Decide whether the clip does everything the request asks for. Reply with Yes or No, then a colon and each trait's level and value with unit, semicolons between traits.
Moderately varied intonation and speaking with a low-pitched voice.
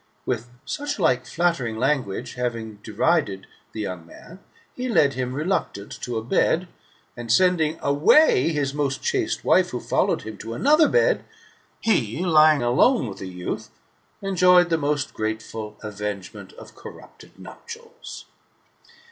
No: wide, 7.7 semitones; low, 130 Hz